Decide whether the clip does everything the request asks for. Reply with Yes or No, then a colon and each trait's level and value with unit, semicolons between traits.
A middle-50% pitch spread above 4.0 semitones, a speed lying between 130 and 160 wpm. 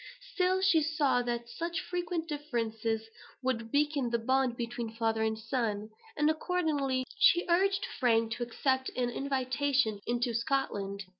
Yes: average, 4.7 semitones; average, 140 wpm